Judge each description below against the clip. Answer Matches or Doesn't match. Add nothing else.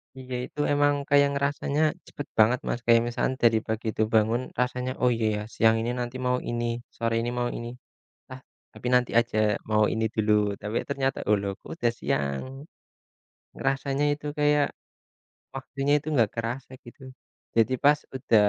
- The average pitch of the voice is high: Doesn't match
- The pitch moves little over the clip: Doesn't match